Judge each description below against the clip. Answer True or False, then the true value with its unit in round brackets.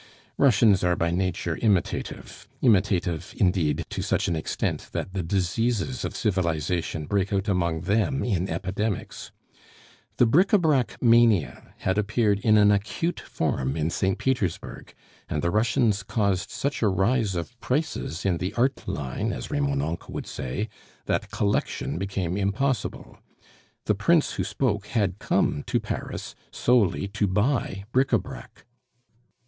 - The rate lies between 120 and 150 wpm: True (145 wpm)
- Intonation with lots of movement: False (4.6 semitones)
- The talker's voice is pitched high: False (100 Hz)